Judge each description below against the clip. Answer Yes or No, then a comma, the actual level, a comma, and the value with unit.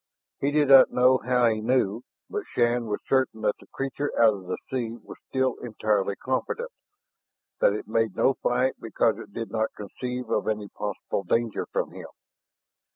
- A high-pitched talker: No, low, 120 Hz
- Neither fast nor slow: Yes, average, 175 wpm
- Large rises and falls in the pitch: No, average, 3.2 semitones